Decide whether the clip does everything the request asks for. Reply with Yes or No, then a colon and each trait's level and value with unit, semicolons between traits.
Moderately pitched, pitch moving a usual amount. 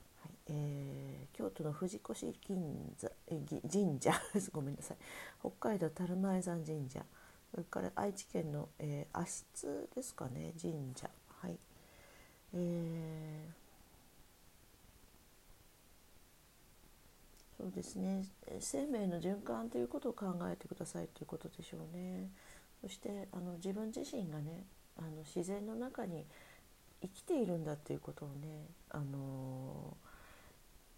Yes: medium, 160 Hz; average, 4.3 semitones